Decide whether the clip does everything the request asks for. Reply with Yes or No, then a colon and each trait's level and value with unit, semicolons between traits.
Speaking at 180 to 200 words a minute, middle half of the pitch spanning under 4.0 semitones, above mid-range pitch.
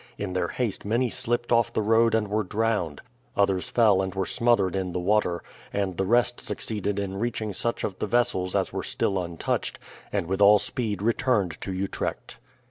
No: average, 190 wpm; average, 3.4 semitones; low, 100 Hz